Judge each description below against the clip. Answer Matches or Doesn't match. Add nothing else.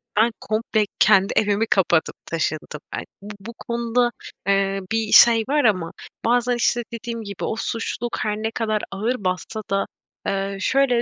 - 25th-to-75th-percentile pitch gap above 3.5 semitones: Doesn't match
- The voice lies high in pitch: Matches